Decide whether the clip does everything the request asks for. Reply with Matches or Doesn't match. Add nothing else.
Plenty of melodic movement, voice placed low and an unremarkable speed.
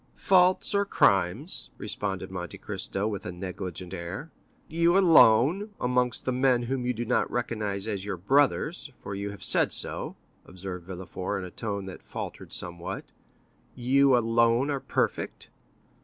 Matches